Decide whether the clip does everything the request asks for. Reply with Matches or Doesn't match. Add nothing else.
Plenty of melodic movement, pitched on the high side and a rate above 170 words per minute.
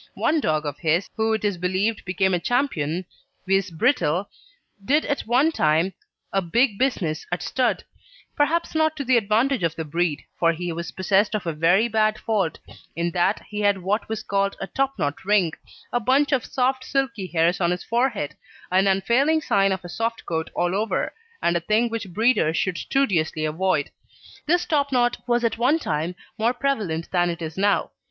Matches